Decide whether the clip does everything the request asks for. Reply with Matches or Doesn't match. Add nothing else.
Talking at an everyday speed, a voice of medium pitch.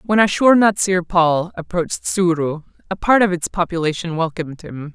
Matches